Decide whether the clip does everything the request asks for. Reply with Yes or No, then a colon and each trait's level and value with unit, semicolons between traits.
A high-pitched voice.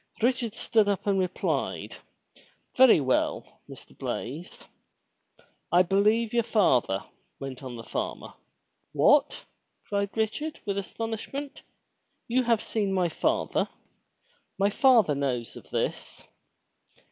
Yes: high, 200 Hz